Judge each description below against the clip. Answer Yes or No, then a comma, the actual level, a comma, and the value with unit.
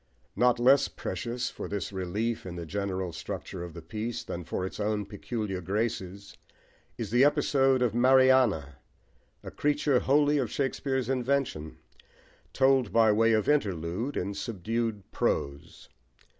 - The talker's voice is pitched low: Yes, low, 110 Hz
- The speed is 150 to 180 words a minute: No, average, 140 wpm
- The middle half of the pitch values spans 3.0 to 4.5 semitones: No, wide, 5.5 semitones